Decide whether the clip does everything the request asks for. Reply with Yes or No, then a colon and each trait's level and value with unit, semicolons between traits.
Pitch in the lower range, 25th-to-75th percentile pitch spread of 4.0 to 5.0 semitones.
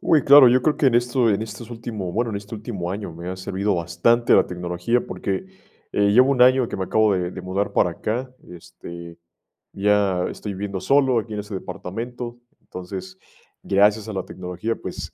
Yes: low, 105 Hz; average, 4.3 semitones